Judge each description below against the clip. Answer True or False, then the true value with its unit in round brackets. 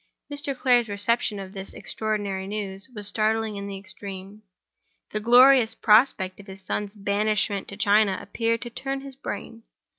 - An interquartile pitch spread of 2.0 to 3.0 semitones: True (2.6 semitones)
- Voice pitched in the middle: False (210 Hz)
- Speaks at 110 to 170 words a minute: True (155 wpm)